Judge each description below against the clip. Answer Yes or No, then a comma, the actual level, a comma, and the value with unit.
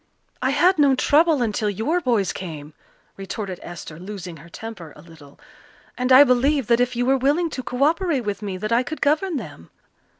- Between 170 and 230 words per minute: Yes, average, 195 wpm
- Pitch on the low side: No, high, 240 Hz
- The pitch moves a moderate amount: No, wide, 7.2 semitones